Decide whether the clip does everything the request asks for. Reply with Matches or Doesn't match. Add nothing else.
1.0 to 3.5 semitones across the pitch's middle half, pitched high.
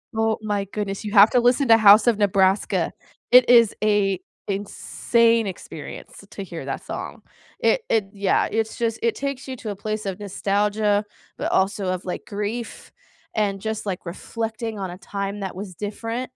Matches